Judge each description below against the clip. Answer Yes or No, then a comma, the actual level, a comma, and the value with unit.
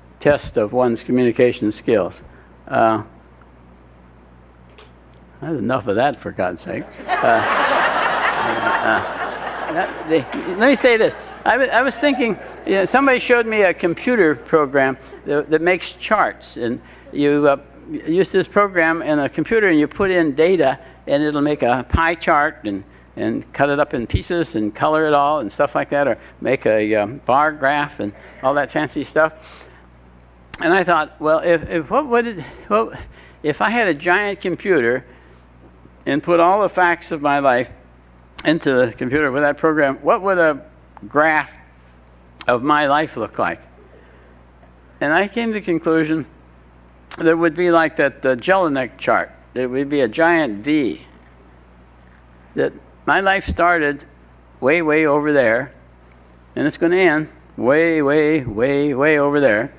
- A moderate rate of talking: Yes, average, 170 wpm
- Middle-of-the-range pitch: Yes, medium, 145 Hz